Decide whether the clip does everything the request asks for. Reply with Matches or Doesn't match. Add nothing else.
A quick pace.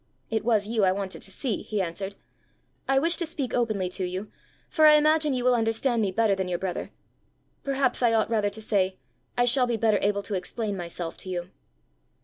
Matches